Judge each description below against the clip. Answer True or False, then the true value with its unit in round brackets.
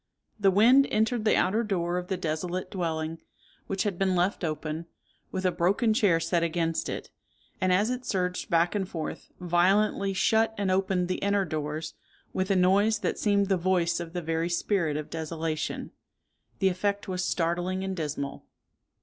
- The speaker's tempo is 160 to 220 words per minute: True (175 wpm)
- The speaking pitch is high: False (180 Hz)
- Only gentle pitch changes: False (3.0 semitones)